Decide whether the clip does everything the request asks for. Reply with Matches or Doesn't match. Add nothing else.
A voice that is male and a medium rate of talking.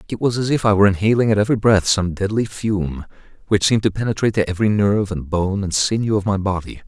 Doesn't match